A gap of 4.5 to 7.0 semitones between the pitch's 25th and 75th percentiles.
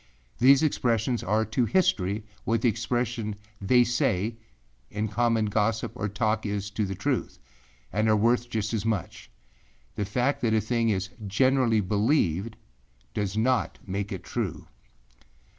No: narrow, 2.6 semitones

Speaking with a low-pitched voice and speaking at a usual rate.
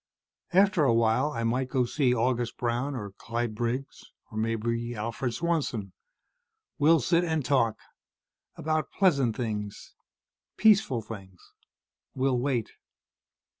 No: low, 120 Hz; slow, 120 wpm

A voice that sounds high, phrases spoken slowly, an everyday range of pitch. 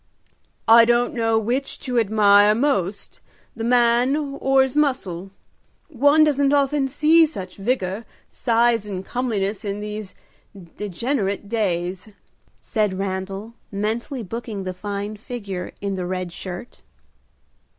Yes: high, 220 Hz; slow, 120 wpm; average, 4.3 semitones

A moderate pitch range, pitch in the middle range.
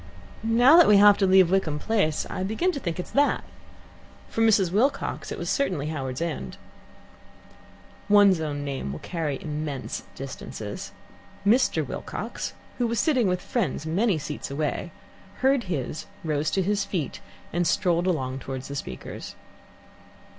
No: wide, 6.1 semitones; medium, 180 Hz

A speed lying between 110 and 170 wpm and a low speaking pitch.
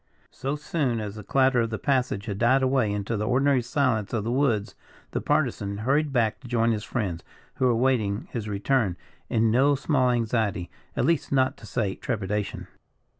No: average, 185 wpm; low, 120 Hz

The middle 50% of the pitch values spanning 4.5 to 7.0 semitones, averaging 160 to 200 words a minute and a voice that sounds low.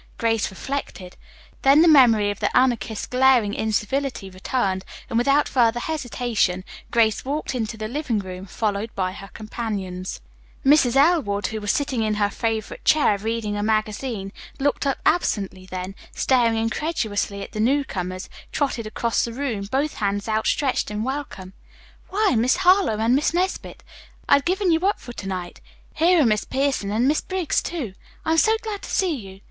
No: wide, 5.5 semitones; average, 170 wpm; high, 230 Hz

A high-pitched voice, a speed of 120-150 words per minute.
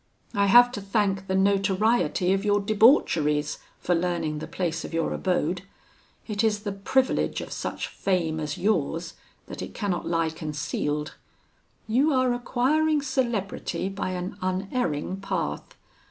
Yes: high, 195 Hz; average, 140 wpm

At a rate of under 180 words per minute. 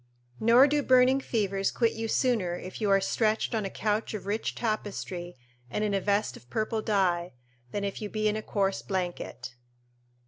No: average, 185 wpm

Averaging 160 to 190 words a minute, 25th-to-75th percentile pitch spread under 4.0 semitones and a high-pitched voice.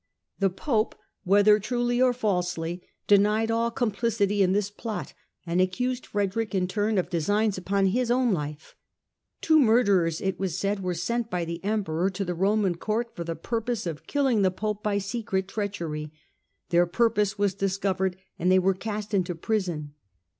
Yes: average, 170 wpm; average, 3.4 semitones; high, 200 Hz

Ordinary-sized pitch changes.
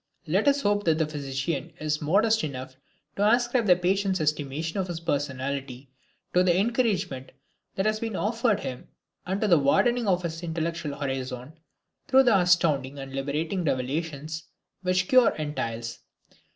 No: wide, 6.0 semitones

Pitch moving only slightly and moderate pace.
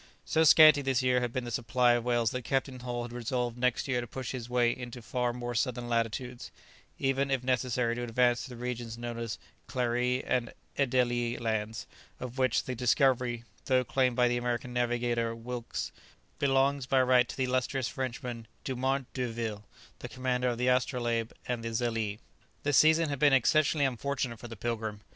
Yes: narrow, 1.6 semitones; average, 185 wpm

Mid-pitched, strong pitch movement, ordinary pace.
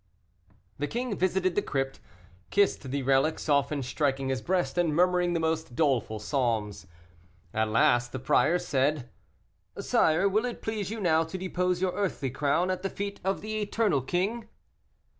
Yes: medium, 165 Hz; wide, 5.8 semitones; average, 160 wpm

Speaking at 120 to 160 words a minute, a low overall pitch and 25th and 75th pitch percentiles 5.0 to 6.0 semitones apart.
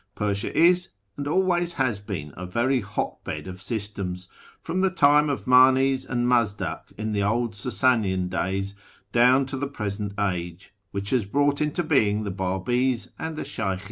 No: average, 170 wpm; low, 115 Hz; wide, 5.5 semitones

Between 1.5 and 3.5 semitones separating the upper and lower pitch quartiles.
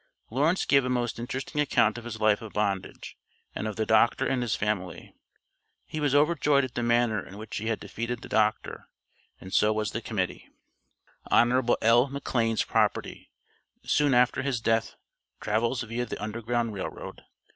Yes: average, 2.8 semitones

